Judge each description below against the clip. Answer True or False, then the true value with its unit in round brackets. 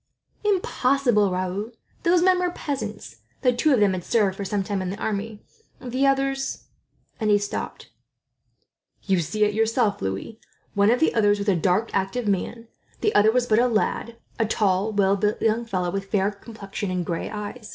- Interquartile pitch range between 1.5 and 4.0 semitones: True (3.6 semitones)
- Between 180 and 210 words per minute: True (190 wpm)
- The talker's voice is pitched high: True (210 Hz)